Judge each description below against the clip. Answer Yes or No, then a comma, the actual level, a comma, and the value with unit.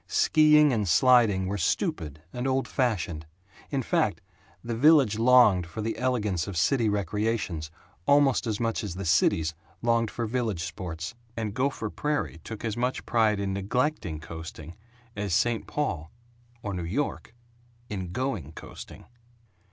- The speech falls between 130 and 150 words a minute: Yes, average, 145 wpm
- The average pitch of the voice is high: No, low, 105 Hz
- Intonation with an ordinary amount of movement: No, wide, 6.0 semitones